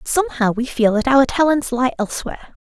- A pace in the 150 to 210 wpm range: Yes, fast, 205 wpm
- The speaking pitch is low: No, very high, 255 Hz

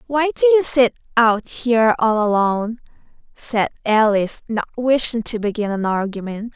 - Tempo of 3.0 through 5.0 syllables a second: Yes, 4.8 syllables/s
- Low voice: No, high, 230 Hz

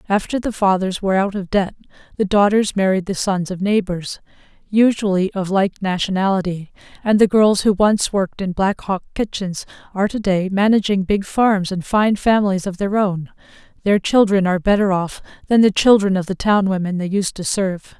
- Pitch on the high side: Yes, high, 195 Hz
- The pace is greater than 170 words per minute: Yes, average, 180 wpm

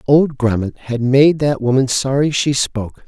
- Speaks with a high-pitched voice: No, low, 130 Hz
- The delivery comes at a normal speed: Yes, average, 175 wpm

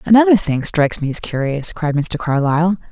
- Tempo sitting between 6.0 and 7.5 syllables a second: No, 5.6 syllables/s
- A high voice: No, medium, 160 Hz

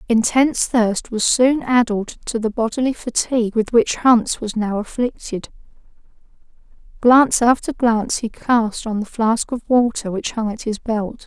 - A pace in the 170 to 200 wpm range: No, average, 160 wpm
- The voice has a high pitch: Yes, high, 230 Hz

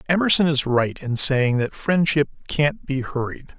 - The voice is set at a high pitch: No, medium, 145 Hz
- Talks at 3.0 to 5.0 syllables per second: Yes, 4.4 syllables/s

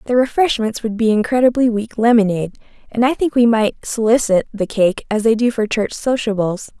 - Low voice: No, high, 225 Hz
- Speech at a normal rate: Yes, average, 185 wpm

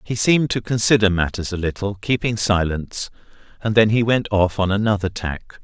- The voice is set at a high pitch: No, low, 105 Hz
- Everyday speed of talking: Yes, average, 180 wpm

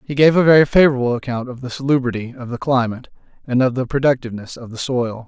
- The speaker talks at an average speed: No, fast, 215 wpm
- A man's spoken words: Yes, male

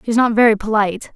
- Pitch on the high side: Yes, high, 220 Hz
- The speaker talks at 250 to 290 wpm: Yes, fast, 260 wpm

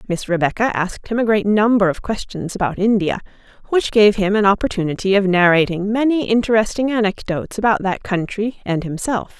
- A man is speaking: No, female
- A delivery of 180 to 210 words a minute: No, average, 165 wpm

